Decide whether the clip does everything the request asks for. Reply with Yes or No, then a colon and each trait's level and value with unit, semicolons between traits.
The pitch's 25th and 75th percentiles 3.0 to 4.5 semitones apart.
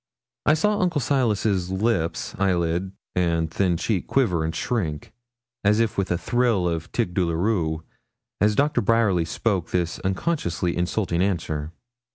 No: average, 5.0 semitones